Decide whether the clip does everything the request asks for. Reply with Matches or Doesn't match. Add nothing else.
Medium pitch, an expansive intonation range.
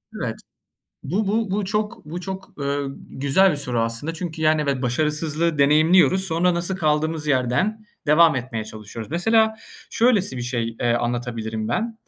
Matches